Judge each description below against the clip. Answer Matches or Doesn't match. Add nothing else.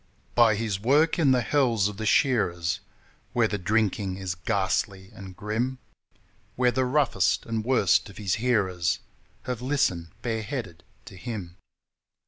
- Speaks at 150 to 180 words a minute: Doesn't match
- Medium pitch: Doesn't match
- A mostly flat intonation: Doesn't match